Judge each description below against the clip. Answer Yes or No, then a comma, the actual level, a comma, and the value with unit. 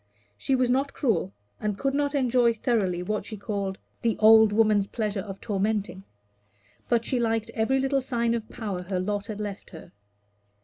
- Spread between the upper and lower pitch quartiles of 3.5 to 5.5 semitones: No, average, 3.1 semitones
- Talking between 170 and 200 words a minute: Yes, average, 175 wpm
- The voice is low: No, high, 220 Hz